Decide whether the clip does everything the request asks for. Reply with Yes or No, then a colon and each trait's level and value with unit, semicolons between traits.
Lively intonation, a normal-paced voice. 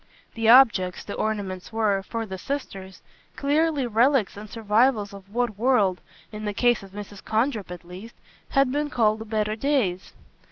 No: average, 3.7 semitones; average, 160 wpm